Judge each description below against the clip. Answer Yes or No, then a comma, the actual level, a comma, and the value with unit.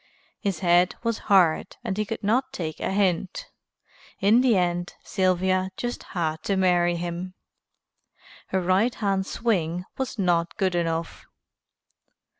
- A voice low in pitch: No, medium, 185 Hz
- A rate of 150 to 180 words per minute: No, slow, 135 wpm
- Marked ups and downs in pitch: No, average, 2.8 semitones